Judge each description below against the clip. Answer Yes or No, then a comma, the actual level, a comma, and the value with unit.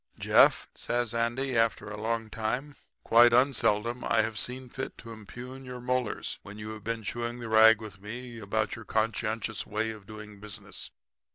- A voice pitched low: Yes, low, 115 Hz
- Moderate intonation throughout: No, narrow, 2.0 semitones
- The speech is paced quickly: No, average, 175 wpm